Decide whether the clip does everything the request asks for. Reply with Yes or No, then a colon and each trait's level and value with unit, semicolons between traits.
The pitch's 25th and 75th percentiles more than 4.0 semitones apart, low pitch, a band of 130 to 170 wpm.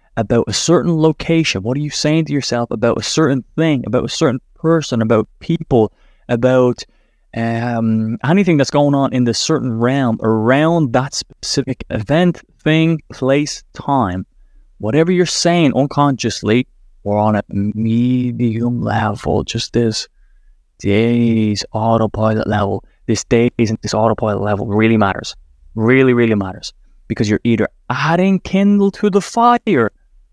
Yes: average, 5.1 semitones; low, 120 Hz; average, 140 wpm